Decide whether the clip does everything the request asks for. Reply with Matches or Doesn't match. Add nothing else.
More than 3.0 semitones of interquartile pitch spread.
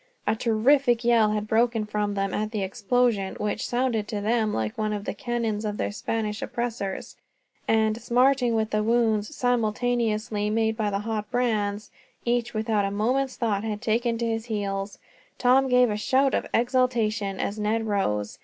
Doesn't match